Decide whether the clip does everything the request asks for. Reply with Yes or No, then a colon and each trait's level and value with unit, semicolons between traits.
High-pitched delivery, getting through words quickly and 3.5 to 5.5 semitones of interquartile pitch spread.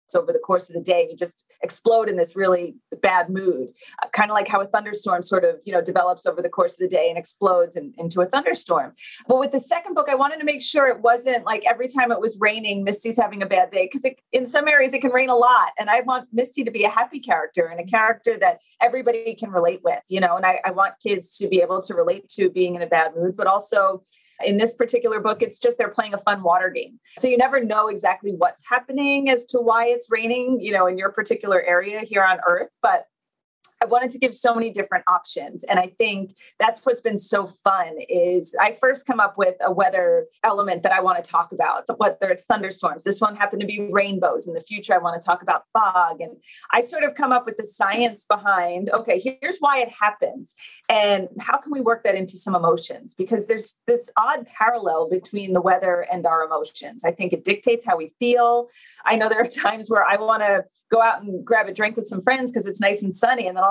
Yes: high, 215 Hz; fast, 245 wpm; average, 5.1 semitones